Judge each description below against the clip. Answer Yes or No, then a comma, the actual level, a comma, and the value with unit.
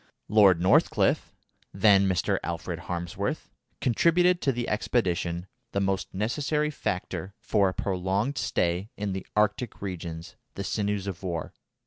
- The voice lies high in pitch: No, low, 100 Hz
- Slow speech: Yes, slow, 130 wpm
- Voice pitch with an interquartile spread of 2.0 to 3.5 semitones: Yes, average, 3.2 semitones